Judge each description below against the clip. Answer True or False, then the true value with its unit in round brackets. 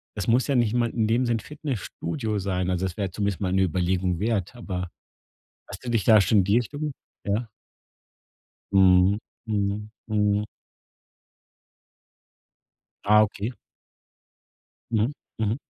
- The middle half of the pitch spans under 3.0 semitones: False (3.4 semitones)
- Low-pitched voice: True (105 Hz)